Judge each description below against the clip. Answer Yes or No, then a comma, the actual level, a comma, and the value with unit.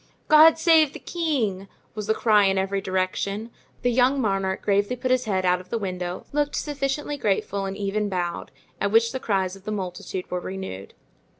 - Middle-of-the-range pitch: No, high, 200 Hz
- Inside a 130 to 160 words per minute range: No, average, 190 wpm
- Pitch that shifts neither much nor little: Yes, average, 5.0 semitones